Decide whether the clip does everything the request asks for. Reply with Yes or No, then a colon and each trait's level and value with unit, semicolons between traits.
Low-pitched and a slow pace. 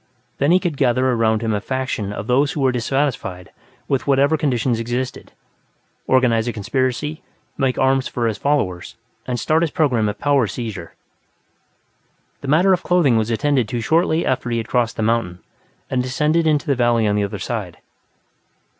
No: low, 125 Hz; average, 175 wpm